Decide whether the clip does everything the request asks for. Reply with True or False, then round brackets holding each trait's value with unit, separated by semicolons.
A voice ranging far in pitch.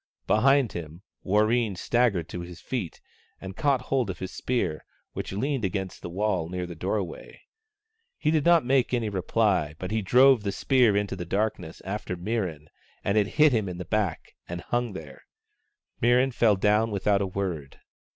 False (4.8 semitones)